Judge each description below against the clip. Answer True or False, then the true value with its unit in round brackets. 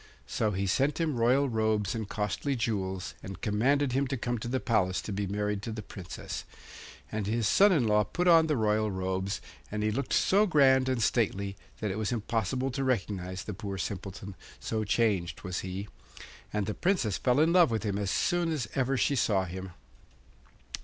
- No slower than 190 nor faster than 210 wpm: True (195 wpm)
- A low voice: True (110 Hz)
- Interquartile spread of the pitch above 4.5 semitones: True (4.9 semitones)